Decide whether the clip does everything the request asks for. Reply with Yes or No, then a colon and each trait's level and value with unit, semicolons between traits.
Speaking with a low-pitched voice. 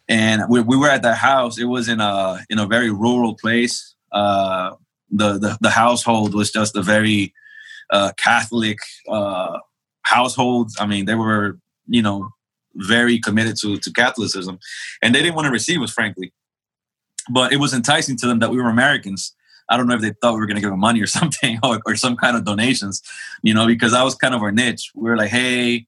Yes: low, 115 Hz